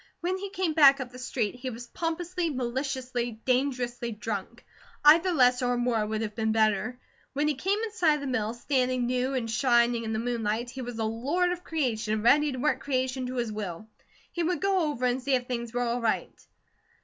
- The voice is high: Yes, very high, 250 Hz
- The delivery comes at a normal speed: No, fast, 210 wpm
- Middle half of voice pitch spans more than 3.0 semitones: Yes, average, 3.7 semitones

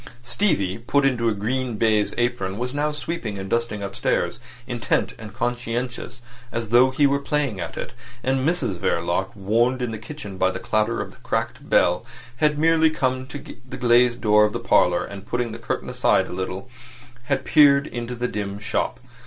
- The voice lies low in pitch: Yes, low, 120 Hz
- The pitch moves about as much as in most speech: Yes, average, 4.0 semitones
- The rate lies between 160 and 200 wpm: Yes, average, 185 wpm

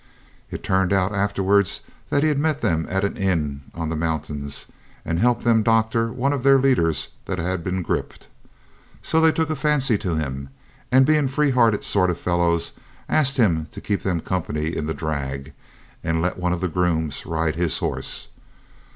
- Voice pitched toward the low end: Yes, very low, 95 Hz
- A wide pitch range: Yes, wide, 6.8 semitones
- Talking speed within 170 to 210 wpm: Yes, average, 185 wpm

